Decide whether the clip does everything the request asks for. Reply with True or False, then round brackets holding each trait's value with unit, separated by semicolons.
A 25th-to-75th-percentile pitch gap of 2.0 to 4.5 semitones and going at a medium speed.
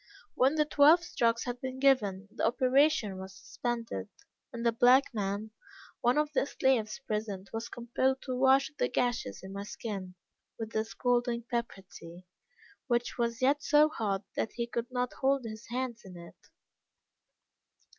True (3.6 semitones; 160 wpm)